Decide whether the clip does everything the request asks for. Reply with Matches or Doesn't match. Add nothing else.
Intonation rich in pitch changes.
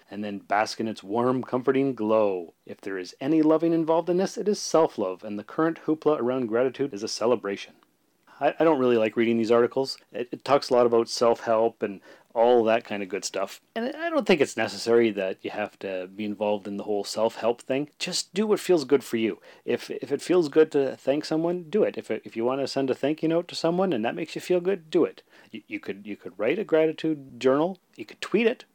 Matches